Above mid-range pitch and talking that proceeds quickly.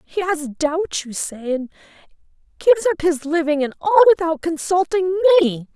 No: very high, 330 Hz; average, 155 wpm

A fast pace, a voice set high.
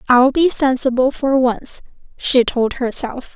No: average, 145 wpm; very high, 255 Hz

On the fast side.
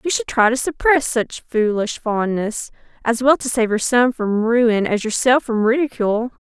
No: average, 185 wpm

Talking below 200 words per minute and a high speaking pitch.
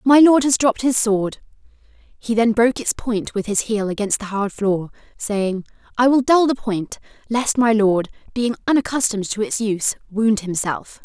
Yes: average, 185 wpm; high, 220 Hz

